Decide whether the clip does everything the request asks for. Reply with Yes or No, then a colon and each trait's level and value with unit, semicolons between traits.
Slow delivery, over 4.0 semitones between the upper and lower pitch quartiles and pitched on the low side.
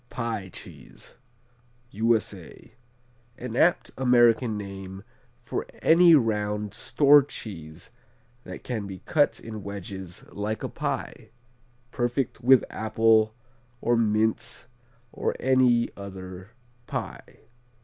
No: slow, 100 wpm; average, 3.4 semitones; low, 110 Hz